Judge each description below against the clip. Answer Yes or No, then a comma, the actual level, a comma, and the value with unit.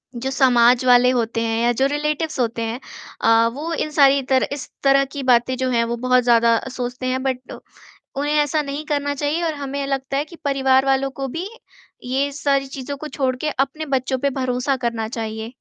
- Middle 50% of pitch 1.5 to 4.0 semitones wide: Yes, narrow, 2.4 semitones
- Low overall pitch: No, very high, 265 Hz